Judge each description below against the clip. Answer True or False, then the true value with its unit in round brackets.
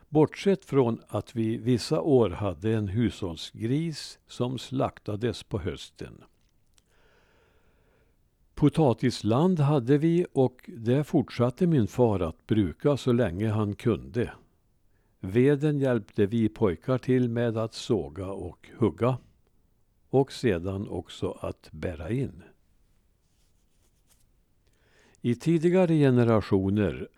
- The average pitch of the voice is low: True (115 Hz)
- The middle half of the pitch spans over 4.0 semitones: True (4.9 semitones)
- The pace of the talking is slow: True (100 wpm)